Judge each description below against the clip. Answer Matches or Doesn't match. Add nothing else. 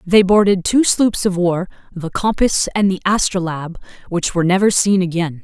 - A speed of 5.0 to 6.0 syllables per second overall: Matches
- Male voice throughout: Doesn't match